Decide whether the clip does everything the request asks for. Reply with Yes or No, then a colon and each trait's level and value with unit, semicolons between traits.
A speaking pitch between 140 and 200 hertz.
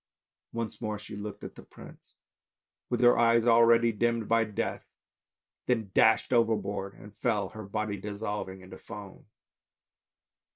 No: low, 110 Hz